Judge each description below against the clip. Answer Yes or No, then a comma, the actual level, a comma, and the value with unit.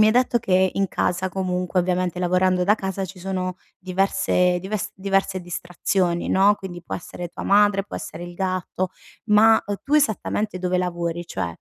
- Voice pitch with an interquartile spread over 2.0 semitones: No, narrow, 1.7 semitones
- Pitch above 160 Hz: Yes, medium, 185 Hz